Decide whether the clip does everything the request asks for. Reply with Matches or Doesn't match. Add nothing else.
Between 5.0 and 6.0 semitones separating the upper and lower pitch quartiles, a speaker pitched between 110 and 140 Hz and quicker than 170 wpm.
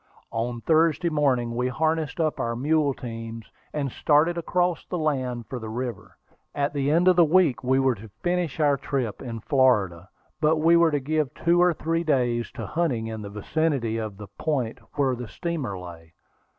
Matches